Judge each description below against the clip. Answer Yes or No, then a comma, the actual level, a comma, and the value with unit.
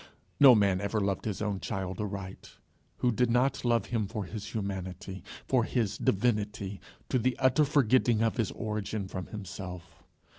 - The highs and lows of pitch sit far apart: No, average, 3.5 semitones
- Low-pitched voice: Yes, low, 105 Hz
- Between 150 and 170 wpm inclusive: Yes, average, 160 wpm